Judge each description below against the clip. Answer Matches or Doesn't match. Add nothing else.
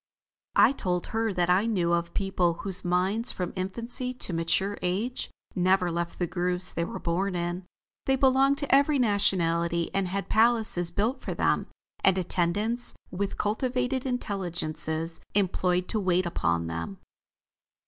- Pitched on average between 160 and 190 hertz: Matches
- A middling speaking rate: Matches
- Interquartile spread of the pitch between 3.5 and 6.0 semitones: Matches